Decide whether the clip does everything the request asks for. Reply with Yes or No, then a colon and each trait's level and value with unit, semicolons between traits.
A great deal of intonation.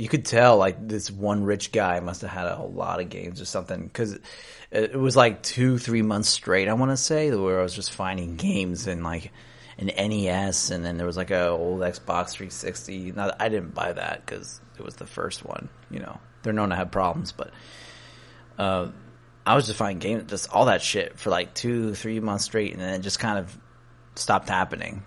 No: average, 3.2 semitones